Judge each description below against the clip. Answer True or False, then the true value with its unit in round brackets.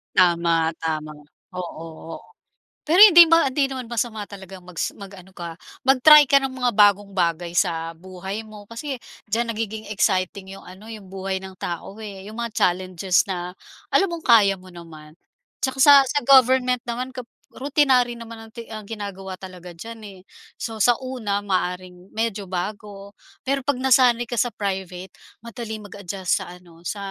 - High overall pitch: True (205 Hz)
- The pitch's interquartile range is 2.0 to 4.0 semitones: False (4.7 semitones)